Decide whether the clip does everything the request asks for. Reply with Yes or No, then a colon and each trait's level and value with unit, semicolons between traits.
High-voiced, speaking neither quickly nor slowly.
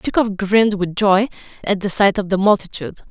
Yes: high, 200 Hz; average, 195 wpm